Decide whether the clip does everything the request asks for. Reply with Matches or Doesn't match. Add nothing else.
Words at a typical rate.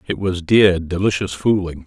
Matches